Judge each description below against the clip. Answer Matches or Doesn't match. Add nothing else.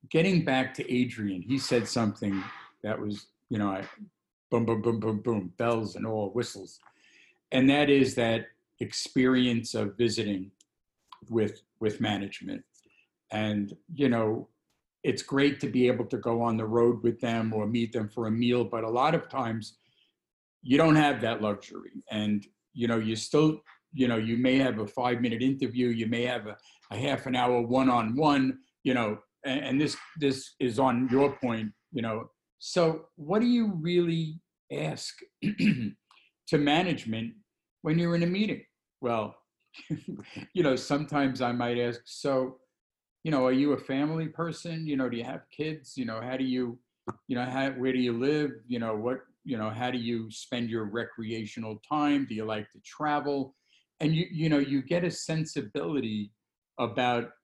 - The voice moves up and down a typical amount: Matches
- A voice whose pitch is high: Doesn't match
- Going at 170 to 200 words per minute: Matches